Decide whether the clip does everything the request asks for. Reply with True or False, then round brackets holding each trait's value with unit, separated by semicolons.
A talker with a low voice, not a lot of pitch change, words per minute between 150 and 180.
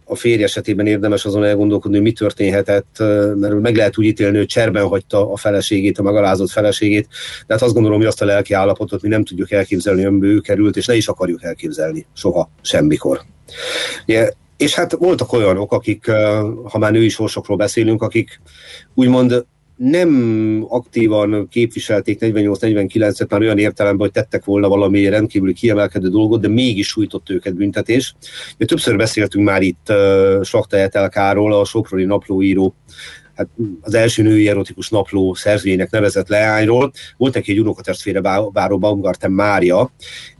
True (105 Hz; 1.6 semitones; 155 wpm)